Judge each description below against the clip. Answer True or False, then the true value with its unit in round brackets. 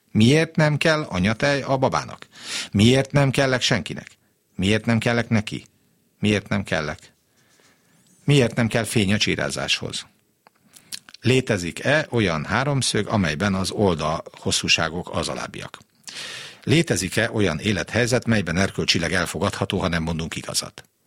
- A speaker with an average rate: True (120 wpm)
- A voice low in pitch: True (110 Hz)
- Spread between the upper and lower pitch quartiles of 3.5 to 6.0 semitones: True (4.9 semitones)